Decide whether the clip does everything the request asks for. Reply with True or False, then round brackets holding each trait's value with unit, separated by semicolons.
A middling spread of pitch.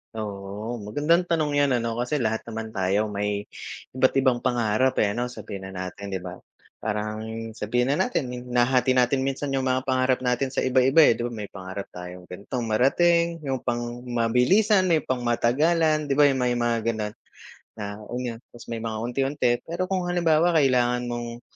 True (3.8 semitones)